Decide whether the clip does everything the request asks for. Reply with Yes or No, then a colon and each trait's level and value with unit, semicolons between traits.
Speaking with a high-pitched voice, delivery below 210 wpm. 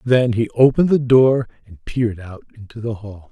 No: low, 115 Hz; average, 200 wpm